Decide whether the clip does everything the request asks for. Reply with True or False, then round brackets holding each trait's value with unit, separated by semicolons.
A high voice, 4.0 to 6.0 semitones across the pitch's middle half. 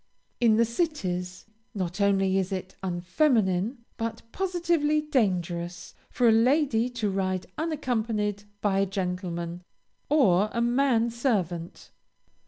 True (210 Hz; 5.2 semitones)